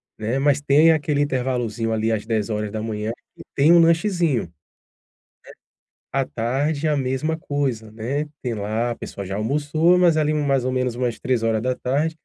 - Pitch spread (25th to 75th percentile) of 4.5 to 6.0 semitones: Yes, average, 4.9 semitones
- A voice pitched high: No, low, 130 Hz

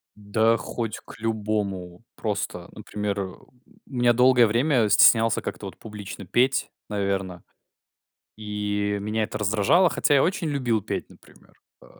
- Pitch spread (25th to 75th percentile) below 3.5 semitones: Yes, average, 2.8 semitones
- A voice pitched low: Yes, low, 110 Hz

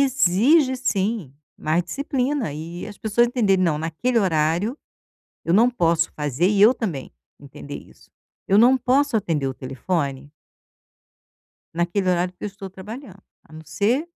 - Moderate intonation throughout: No, wide, 6.6 semitones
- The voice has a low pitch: No, high, 190 Hz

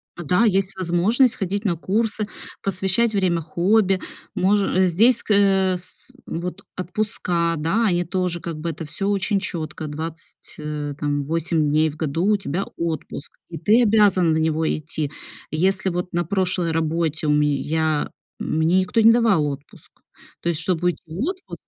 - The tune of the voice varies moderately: Yes, average, 3.6 semitones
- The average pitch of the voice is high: No, medium, 175 Hz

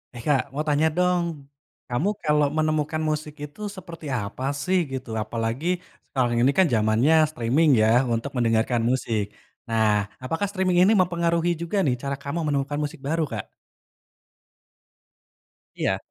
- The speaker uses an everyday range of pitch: No, wide, 5.7 semitones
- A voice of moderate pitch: Yes, medium, 145 Hz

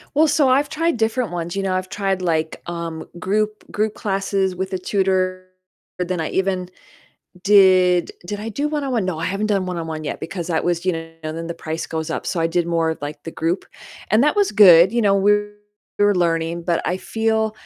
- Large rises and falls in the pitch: No, average, 3.7 semitones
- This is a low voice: No, medium, 185 Hz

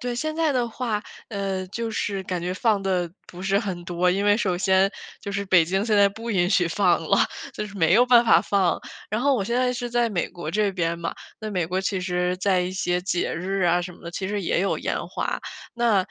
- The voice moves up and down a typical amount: Yes, average, 3.2 semitones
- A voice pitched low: No, high, 195 Hz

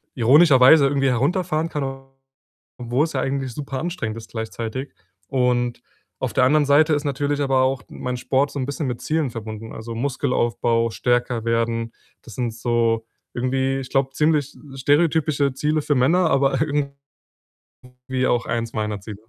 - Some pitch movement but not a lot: Yes, average, 3.4 semitones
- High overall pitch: No, low, 130 Hz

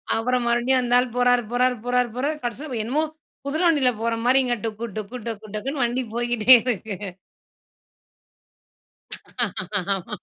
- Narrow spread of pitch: Yes, narrow, 1.8 semitones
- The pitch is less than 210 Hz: No, high, 245 Hz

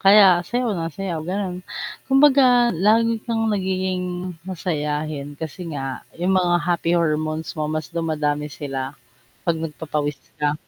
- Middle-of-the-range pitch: Yes, medium, 170 Hz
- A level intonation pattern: No, average, 4.0 semitones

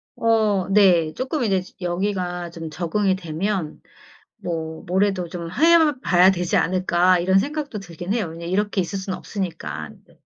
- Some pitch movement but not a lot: Yes, average, 3.0 semitones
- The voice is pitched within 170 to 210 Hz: Yes, medium, 185 Hz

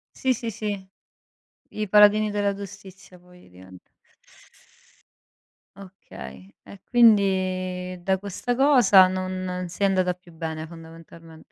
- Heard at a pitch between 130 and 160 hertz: No, medium, 185 Hz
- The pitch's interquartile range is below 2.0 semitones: No, narrow, 2.4 semitones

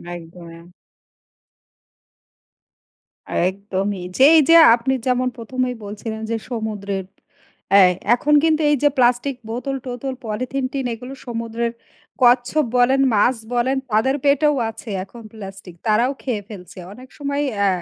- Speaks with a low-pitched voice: No, high, 240 Hz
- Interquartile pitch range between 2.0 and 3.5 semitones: No, average, 4.1 semitones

